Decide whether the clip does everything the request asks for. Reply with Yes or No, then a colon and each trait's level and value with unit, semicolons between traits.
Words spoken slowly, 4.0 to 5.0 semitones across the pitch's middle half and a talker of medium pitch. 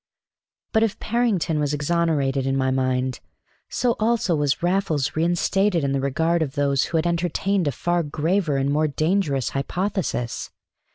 No: average, 155 wpm; average, 4.6 semitones; medium, 160 Hz